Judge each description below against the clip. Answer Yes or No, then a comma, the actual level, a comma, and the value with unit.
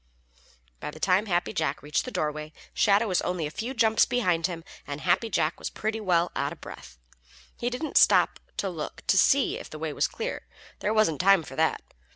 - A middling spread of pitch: No, wide, 5.7 semitones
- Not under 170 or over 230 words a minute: Yes, fast, 205 wpm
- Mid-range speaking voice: Yes, medium, 180 Hz